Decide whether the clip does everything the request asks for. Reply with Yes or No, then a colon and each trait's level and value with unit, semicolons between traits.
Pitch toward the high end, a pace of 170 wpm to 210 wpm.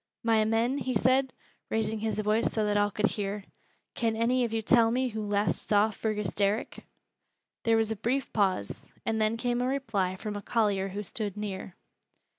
Yes: high, 220 Hz; average, 190 wpm